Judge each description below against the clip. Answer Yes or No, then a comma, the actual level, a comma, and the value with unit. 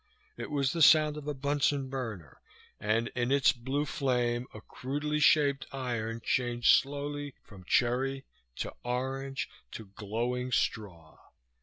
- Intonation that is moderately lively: Yes, average, 3.0 semitones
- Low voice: Yes, low, 130 Hz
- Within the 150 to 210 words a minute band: No, slow, 135 wpm